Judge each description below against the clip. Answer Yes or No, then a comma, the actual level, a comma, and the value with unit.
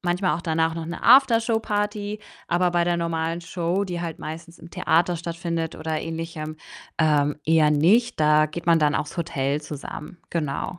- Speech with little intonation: Yes, narrow, 2.0 semitones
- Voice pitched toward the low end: No, medium, 165 Hz